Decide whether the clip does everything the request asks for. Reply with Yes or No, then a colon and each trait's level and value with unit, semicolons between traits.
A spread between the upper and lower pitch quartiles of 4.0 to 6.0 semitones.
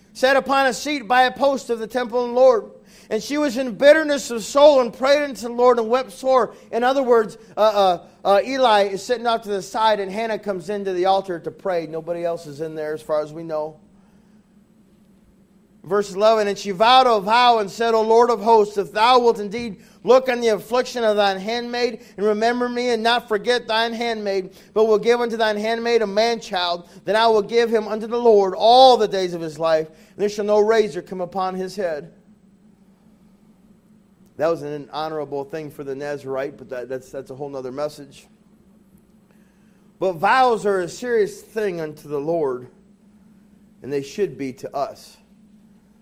No: average, 3.5 semitones